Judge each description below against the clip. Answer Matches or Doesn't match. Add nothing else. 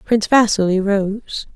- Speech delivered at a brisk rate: Doesn't match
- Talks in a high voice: Matches